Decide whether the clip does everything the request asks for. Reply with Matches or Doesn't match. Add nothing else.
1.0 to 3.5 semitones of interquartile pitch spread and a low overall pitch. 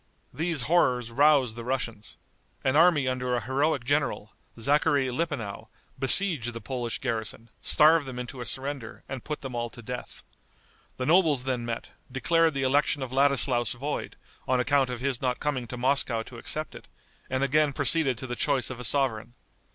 Matches